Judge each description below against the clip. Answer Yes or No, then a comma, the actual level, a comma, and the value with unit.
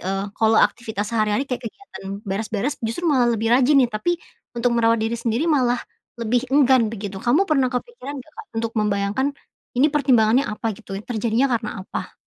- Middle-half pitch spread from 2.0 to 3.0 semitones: No, average, 3.6 semitones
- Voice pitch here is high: Yes, high, 235 Hz